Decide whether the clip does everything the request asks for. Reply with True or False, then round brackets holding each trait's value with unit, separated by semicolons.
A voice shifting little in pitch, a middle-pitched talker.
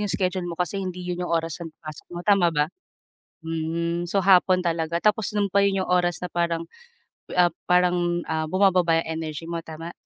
True (1.8 semitones; 175 Hz)